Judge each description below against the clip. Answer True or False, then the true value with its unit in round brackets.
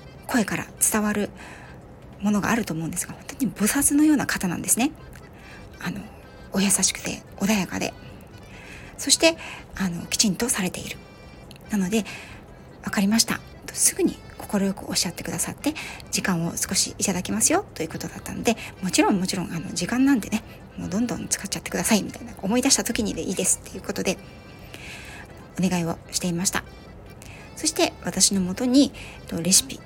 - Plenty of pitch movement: False (4.3 semitones)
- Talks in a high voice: True (205 Hz)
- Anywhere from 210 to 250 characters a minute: False (370 characters per minute)